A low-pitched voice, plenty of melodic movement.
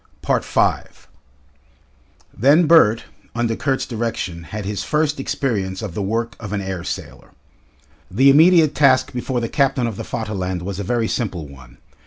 Yes: low, 115 Hz; wide, 5.8 semitones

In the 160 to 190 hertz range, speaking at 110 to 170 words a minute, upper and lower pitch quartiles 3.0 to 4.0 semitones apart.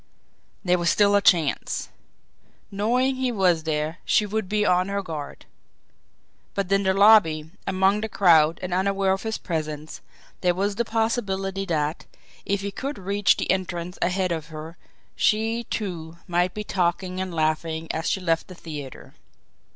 Yes: medium, 185 Hz; average, 160 wpm; average, 3.5 semitones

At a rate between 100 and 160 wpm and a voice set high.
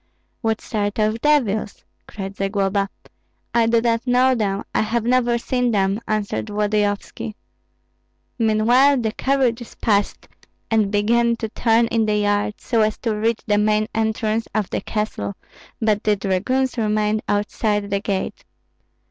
Yes: average, 145 wpm; high, 215 Hz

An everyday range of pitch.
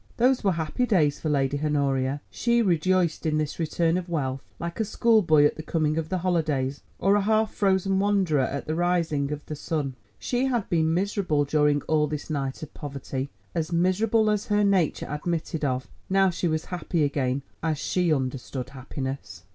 Yes: average, 4.5 semitones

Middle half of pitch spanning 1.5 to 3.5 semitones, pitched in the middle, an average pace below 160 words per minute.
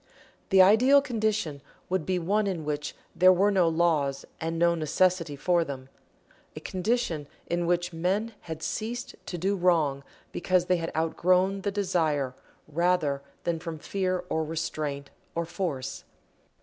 Yes: average, 3.2 semitones; medium, 175 Hz; average, 150 wpm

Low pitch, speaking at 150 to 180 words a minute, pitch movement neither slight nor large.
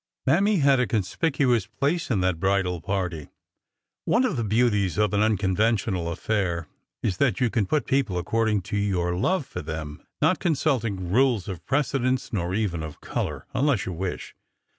No: low, 105 Hz; average, 165 wpm; wide, 5.9 semitones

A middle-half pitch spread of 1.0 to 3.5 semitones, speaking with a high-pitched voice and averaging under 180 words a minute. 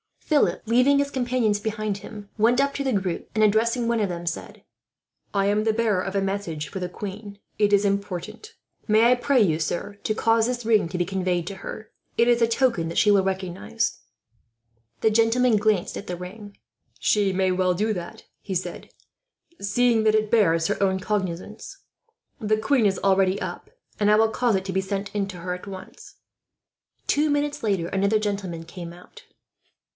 No: average, 3.2 semitones; high, 205 Hz; average, 195 wpm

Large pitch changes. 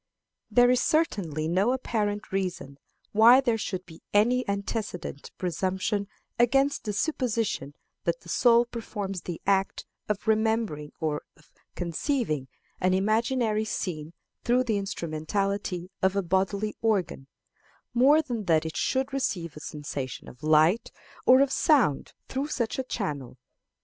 Yes: wide, 5.9 semitones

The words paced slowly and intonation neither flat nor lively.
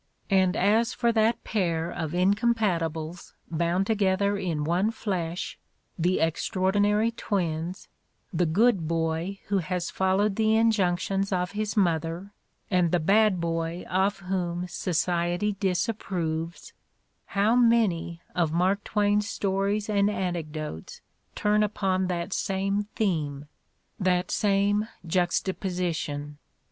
Yes: slow, 115 wpm; average, 3.2 semitones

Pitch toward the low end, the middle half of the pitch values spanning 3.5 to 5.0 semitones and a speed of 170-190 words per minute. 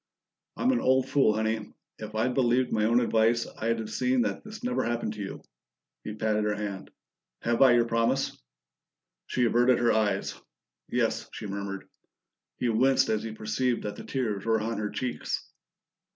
No: low, 115 Hz; narrow, 2.5 semitones; average, 175 wpm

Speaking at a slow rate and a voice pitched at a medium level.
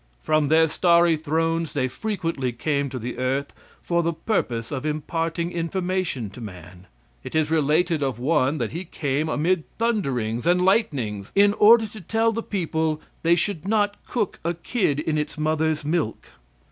No: average, 165 wpm; medium, 160 Hz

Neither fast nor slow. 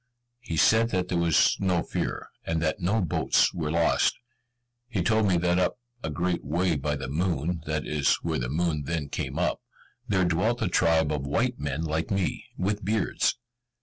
Yes: average, 185 wpm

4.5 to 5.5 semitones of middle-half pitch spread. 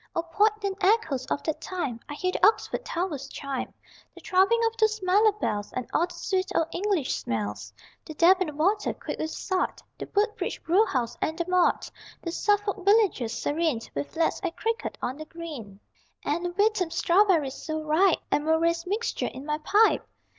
Yes: average, 5.1 semitones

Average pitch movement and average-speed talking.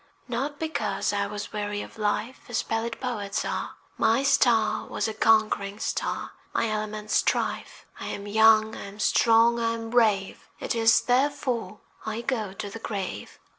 No: narrow, 2.0 semitones; average, 165 wpm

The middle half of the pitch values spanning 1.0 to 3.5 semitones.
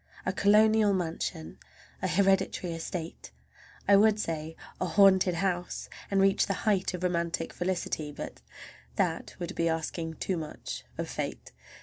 Yes: average, 3.0 semitones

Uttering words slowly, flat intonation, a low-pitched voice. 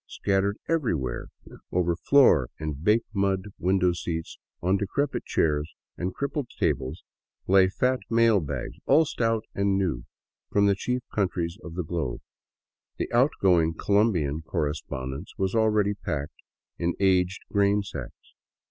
No: slow, 130 wpm; average, 4.4 semitones; very low, 95 Hz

